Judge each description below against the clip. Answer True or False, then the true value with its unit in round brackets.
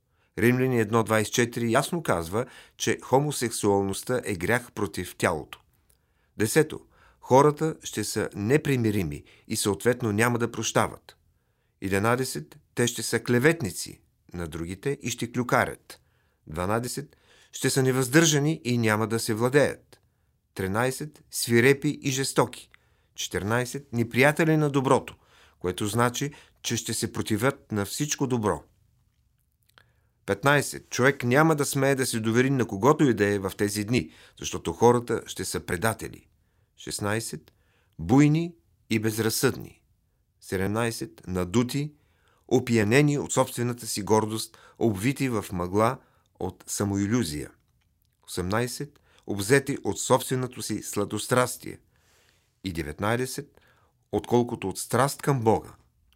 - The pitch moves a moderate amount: True (4.2 semitones)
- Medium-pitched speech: False (115 Hz)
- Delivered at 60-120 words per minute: True (115 wpm)